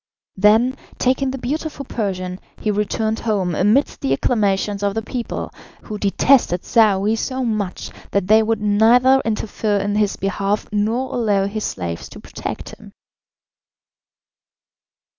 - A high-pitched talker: Yes, high, 210 Hz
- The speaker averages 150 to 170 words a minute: No, slow, 135 wpm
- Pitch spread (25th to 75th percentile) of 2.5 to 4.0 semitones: Yes, average, 2.8 semitones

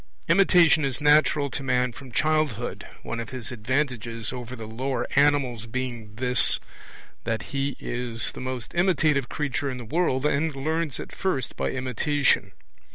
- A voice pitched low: Yes, low, 130 Hz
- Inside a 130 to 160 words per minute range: Yes, average, 155 wpm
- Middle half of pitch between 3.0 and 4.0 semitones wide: Yes, average, 3.4 semitones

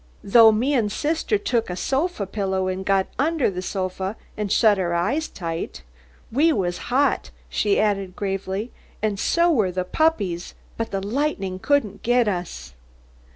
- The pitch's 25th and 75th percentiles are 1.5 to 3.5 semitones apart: No, average, 5.2 semitones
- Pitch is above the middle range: Yes, high, 205 Hz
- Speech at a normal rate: Yes, average, 155 wpm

